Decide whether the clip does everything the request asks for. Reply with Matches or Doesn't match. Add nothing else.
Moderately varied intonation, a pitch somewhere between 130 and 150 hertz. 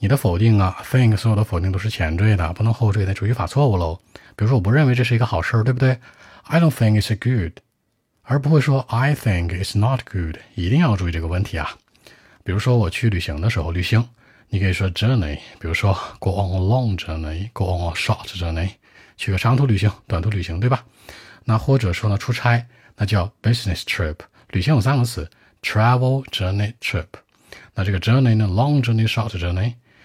Doesn't match